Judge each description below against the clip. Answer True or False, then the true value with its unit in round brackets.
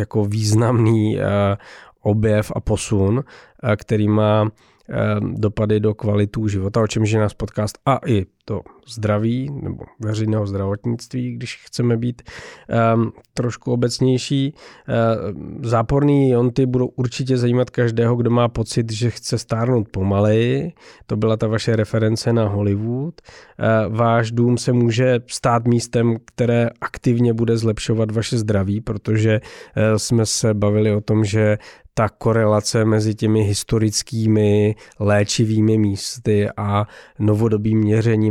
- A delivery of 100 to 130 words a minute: True (125 wpm)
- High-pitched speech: False (110 Hz)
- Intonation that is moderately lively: False (2.1 semitones)